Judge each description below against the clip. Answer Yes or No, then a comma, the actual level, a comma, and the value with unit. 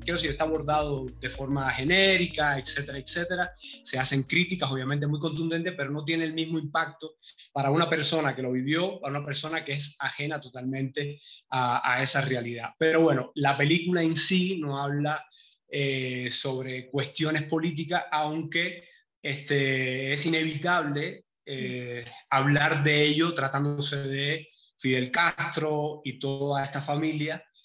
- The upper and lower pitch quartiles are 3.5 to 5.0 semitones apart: No, average, 2.9 semitones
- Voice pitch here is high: No, medium, 150 Hz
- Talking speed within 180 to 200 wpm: No, average, 145 wpm